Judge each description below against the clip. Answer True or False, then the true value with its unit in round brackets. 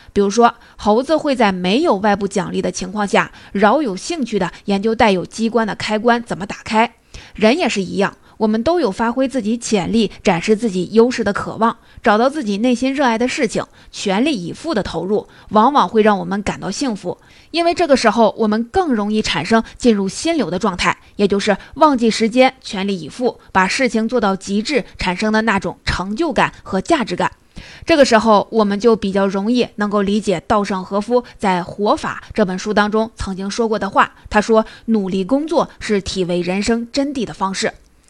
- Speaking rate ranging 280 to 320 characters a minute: True (295 characters per minute)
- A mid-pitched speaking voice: False (215 Hz)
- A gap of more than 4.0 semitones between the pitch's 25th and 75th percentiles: False (3.2 semitones)